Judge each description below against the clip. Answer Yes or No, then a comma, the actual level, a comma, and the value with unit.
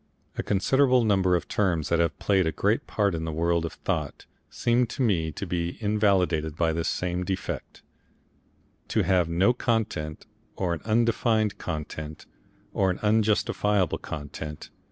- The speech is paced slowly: No, average, 155 wpm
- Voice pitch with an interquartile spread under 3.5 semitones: No, average, 4.4 semitones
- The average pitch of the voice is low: Yes, very low, 90 Hz